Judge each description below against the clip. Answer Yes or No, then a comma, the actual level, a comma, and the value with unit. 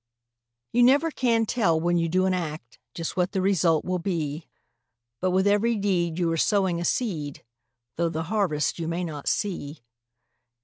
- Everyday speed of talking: Yes, average, 175 wpm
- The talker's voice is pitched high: No, medium, 175 Hz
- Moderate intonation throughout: Yes, average, 3.6 semitones